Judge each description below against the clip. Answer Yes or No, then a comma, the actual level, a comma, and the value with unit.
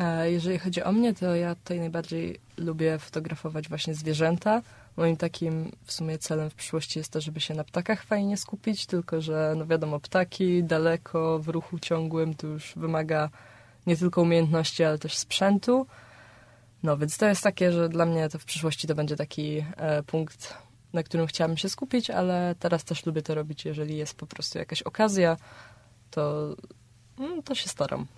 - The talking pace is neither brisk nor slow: No, fast, 170 wpm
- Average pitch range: No, narrow, 2.3 semitones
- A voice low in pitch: No, medium, 160 Hz